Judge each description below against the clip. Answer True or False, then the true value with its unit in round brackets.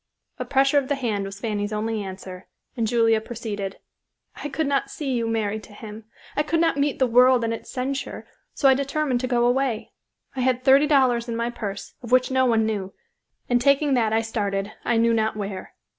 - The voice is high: True (235 Hz)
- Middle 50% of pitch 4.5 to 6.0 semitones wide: False (3.5 semitones)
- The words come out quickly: True (210 wpm)